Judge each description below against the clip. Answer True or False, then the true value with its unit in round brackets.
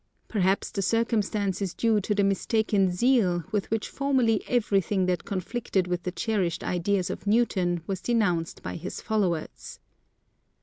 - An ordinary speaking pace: True (145 wpm)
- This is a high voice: True (200 Hz)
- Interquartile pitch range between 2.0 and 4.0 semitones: True (3.5 semitones)